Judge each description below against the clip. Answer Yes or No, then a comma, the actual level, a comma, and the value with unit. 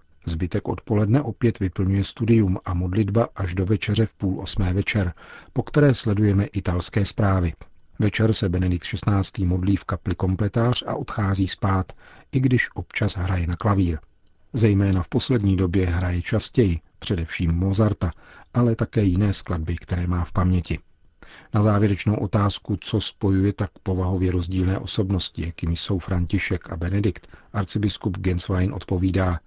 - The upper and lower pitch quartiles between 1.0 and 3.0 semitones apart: Yes, average, 2.7 semitones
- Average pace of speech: Yes, average, 140 wpm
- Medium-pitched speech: No, very low, 95 Hz